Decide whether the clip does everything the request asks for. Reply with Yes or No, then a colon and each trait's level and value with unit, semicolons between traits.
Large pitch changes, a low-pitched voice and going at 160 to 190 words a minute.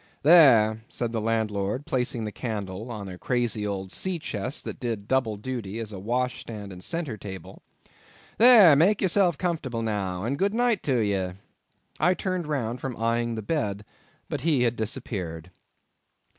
Yes: wide, 5.8 semitones; low, 115 Hz; average, 165 wpm